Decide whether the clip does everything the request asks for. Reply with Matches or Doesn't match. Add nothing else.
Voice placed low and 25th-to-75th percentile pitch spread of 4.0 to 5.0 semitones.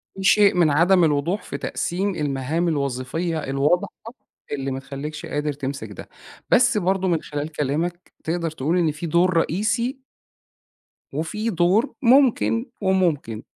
Doesn't match